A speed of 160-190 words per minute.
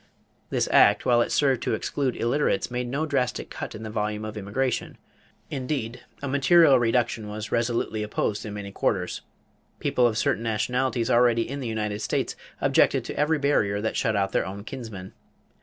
Yes: average, 175 wpm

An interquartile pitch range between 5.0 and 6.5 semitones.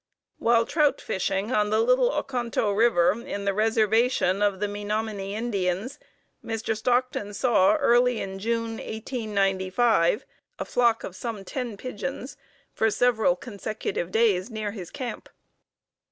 No: average, 3.2 semitones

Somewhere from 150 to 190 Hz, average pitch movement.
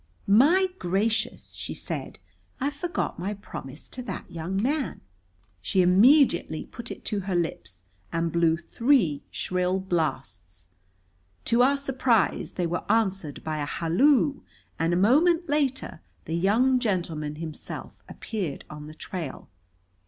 No: medium, 185 Hz; wide, 7.6 semitones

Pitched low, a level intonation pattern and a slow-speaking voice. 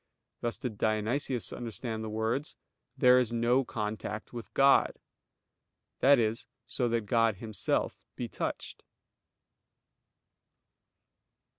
Yes: low, 115 Hz; narrow, 2.3 semitones; slow, 105 wpm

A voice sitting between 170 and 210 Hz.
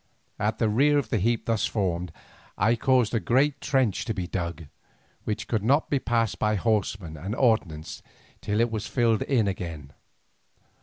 No: low, 110 Hz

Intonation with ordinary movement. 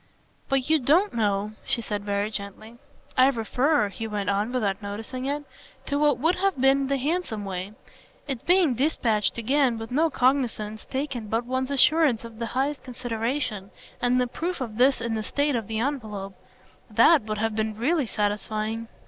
Yes: average, 4.4 semitones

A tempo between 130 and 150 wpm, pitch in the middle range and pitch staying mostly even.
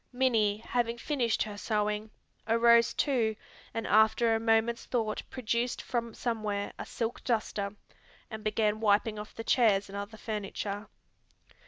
No: average, 140 wpm; high, 220 Hz; narrow, 1.8 semitones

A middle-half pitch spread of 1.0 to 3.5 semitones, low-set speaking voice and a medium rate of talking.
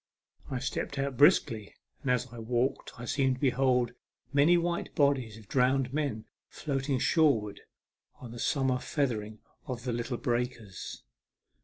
Yes: average, 2.8 semitones; low, 125 Hz; average, 155 wpm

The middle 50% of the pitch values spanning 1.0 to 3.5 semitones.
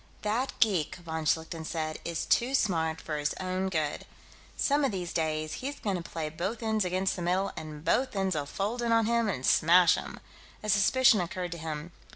No: average, 4.9 semitones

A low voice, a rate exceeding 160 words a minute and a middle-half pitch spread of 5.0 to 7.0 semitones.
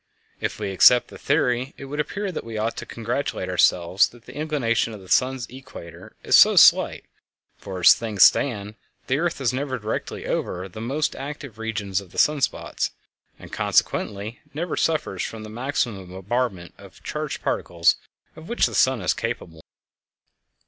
Yes: low, 115 Hz; average, 170 wpm; wide, 5.6 semitones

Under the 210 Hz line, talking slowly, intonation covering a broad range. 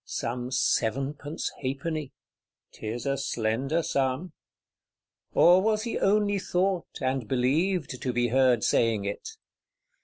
Yes: low, 135 Hz; slow, 115 wpm; wide, 6.0 semitones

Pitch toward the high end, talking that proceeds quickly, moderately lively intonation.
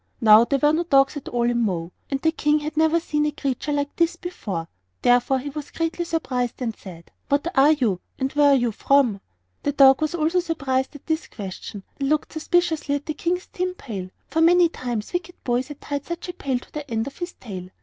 Yes: very high, 285 Hz; fast, 230 wpm; average, 4.7 semitones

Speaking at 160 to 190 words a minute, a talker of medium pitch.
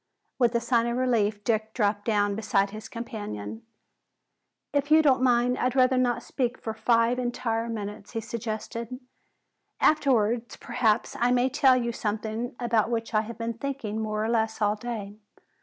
No: average, 165 wpm; high, 230 Hz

